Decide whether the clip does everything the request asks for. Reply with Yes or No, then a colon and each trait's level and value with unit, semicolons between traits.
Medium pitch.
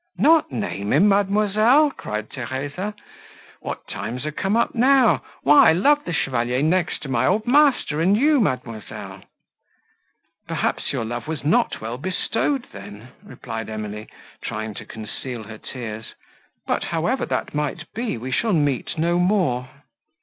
Yes: medium, 150 Hz